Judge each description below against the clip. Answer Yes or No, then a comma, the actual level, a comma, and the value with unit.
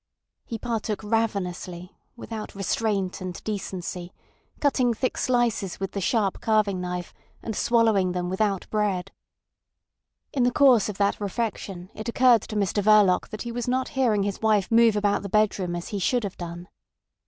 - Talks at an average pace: Yes, average, 165 wpm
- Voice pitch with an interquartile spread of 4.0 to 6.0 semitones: No, average, 3.4 semitones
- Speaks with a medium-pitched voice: No, high, 210 Hz